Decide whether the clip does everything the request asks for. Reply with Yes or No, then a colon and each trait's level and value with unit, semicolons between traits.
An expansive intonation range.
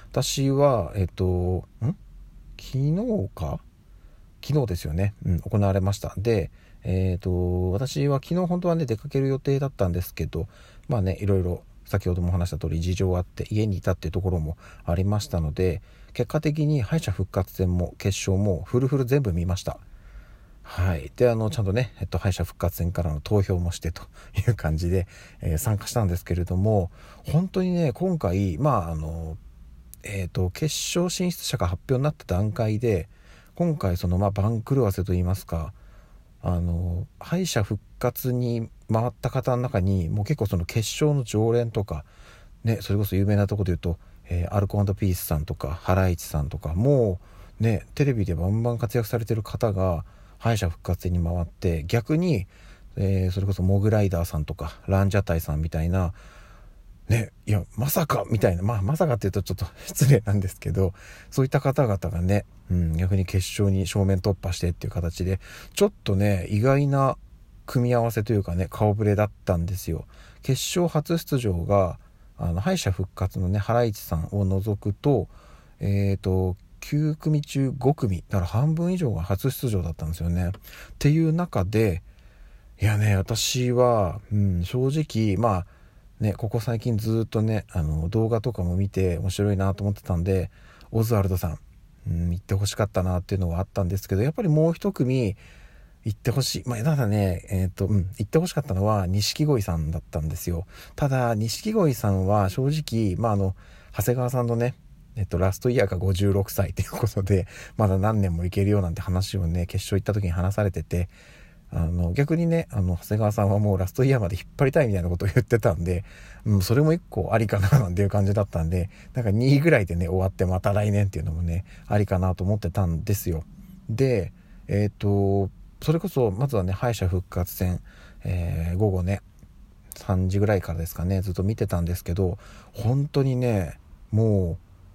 No: average, 4.6 semitones